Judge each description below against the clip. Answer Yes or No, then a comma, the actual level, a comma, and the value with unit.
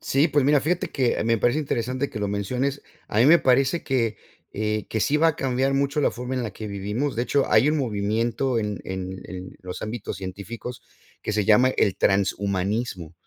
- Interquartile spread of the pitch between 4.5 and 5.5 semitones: Yes, average, 4.8 semitones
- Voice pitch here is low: Yes, low, 115 Hz